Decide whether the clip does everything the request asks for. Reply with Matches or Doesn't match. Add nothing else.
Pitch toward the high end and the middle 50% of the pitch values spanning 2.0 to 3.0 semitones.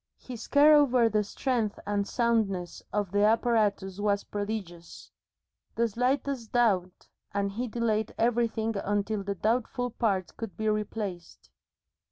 Matches